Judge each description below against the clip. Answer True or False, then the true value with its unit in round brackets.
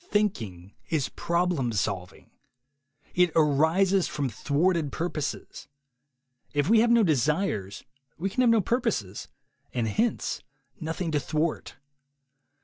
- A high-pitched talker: False (160 Hz)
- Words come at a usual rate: False (120 wpm)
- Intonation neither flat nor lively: False (6.0 semitones)